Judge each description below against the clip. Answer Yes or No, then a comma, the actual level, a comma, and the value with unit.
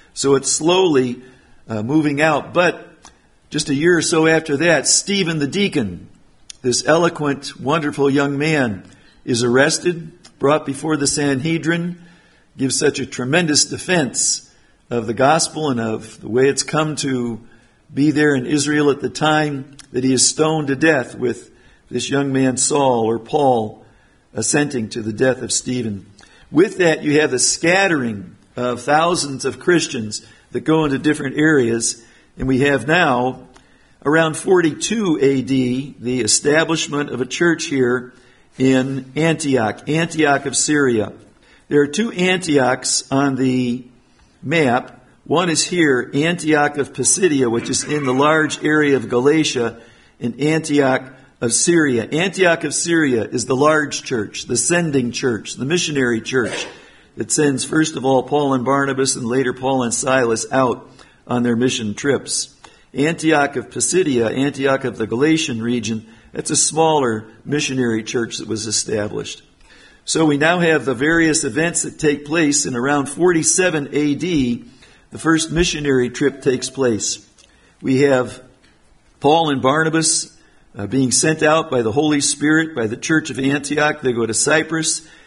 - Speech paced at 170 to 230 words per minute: No, average, 150 wpm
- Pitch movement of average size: Yes, average, 3.8 semitones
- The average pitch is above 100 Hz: Yes, medium, 140 Hz